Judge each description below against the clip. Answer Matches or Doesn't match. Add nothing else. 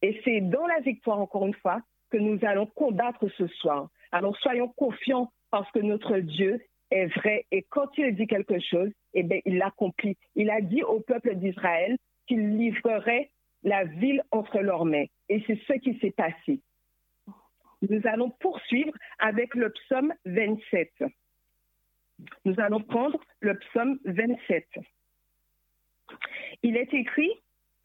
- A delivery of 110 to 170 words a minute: Matches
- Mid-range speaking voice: Doesn't match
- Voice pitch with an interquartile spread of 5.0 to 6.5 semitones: Doesn't match